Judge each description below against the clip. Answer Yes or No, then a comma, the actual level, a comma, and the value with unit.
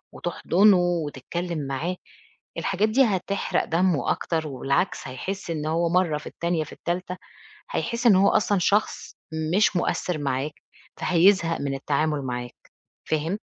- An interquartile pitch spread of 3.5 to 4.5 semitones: Yes, average, 4.0 semitones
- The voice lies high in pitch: No, medium, 170 Hz